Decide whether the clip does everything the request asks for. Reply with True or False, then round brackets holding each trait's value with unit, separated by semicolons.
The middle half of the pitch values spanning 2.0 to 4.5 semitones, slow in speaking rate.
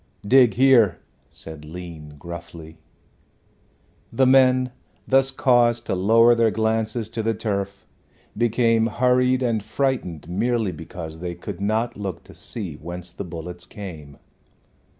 False (5.6 semitones; 130 wpm)